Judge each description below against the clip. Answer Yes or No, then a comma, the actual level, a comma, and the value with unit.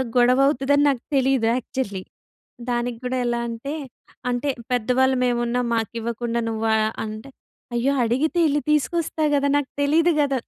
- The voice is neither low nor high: No, very high, 250 Hz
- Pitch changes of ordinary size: Yes, average, 3.1 semitones